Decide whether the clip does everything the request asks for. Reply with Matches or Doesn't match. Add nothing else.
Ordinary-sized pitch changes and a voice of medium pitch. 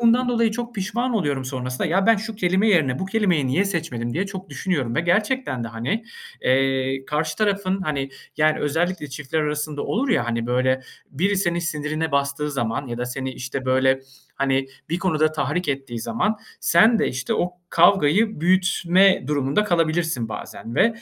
Doesn't match